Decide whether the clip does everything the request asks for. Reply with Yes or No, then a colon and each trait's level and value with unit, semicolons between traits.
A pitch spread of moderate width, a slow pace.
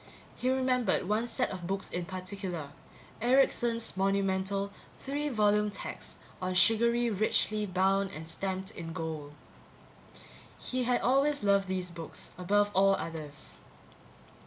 Yes: average, 3.9 semitones; slow, 125 wpm